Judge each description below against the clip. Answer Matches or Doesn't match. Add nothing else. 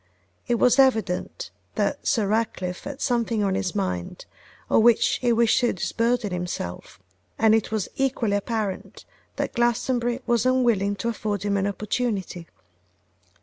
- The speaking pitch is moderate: Doesn't match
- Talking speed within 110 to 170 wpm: Matches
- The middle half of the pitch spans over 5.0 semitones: Doesn't match